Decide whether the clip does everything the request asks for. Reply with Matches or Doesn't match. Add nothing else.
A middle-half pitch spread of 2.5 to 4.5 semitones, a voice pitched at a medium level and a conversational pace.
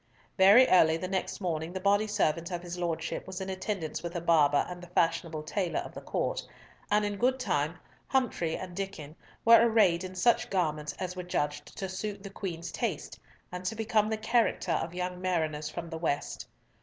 Matches